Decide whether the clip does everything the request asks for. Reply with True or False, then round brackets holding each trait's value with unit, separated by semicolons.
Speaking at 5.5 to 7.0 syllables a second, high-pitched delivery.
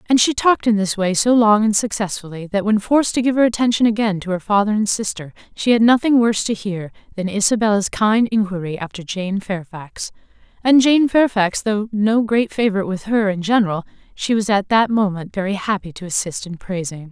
True (5.6 syllables/s; 210 Hz)